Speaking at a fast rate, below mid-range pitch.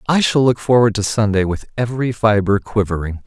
No: average, 185 wpm; low, 110 Hz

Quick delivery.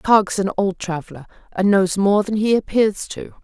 No: average, 190 wpm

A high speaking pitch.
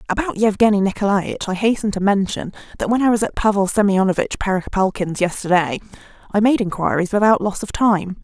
Yes: high, 200 Hz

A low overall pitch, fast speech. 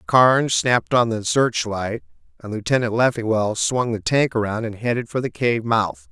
No: low, 115 Hz; average, 185 wpm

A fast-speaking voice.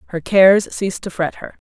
Yes: fast, 215 wpm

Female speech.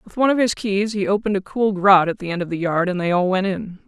Yes: female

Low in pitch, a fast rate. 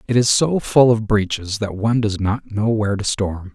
Yes: low, 105 Hz; fast, 235 wpm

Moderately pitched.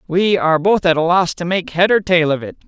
Yes: medium, 175 Hz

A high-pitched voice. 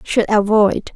Yes: high, 210 Hz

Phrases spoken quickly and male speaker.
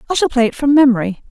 No: fast, 275 wpm; female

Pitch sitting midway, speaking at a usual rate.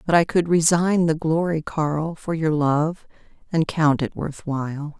Yes: medium, 160 Hz; average, 180 wpm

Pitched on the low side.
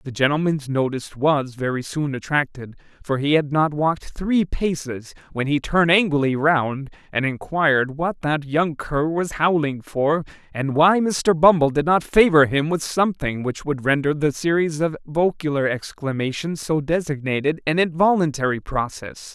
No: medium, 150 Hz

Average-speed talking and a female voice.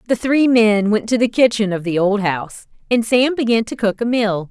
No: fast, 240 wpm; female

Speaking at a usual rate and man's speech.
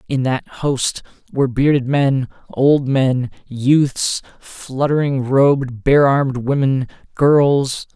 No: slow, 115 wpm; male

